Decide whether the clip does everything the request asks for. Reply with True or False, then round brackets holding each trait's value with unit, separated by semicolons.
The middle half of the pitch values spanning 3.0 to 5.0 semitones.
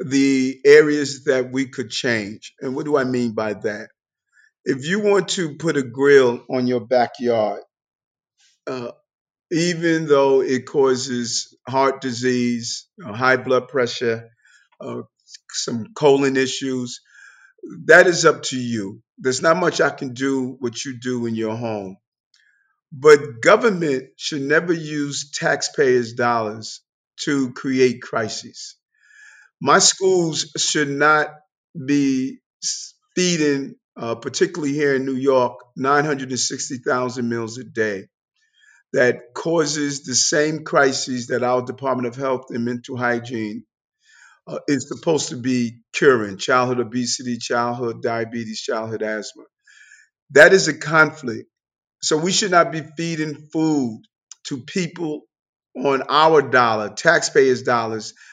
True (4.1 semitones)